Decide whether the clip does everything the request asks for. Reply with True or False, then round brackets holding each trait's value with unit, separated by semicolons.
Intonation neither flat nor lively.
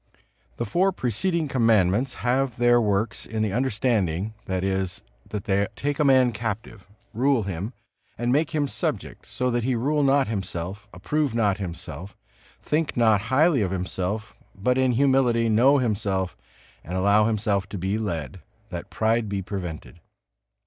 True (4.8 semitones)